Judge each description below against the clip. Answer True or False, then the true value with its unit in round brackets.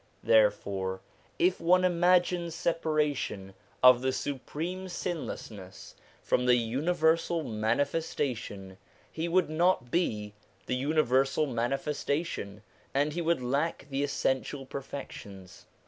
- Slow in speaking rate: True (105 wpm)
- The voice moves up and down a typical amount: False (6.3 semitones)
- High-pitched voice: False (140 Hz)